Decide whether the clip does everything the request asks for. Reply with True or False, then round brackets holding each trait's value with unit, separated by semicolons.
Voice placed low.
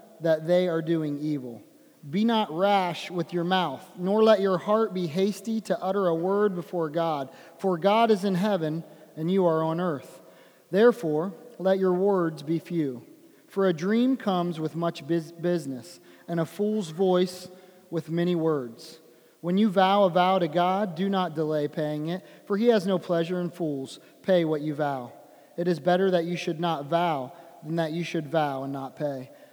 False (175 Hz)